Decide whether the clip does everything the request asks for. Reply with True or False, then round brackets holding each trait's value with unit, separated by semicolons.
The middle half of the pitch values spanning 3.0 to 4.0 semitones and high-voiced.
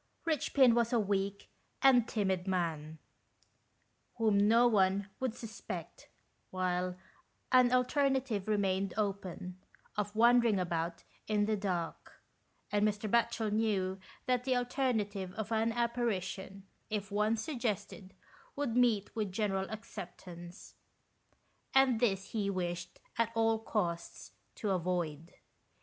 True (3.7 semitones; 210 Hz)